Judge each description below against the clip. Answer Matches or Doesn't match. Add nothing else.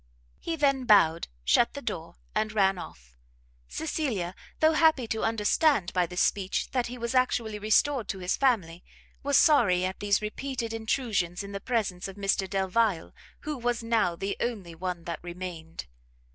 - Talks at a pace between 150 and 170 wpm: Matches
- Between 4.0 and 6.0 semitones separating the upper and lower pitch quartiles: Matches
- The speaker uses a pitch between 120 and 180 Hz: Doesn't match